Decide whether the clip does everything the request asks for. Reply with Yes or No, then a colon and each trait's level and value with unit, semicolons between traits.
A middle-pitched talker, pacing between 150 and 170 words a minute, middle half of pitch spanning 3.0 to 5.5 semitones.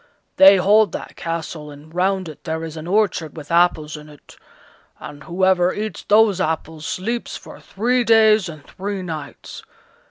Yes: medium, 175 Hz; average, 160 wpm; average, 4.4 semitones